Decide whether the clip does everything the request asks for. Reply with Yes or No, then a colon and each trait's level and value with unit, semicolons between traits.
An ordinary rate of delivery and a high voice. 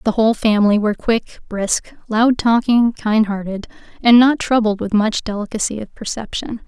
Yes: average, 160 wpm; high, 220 Hz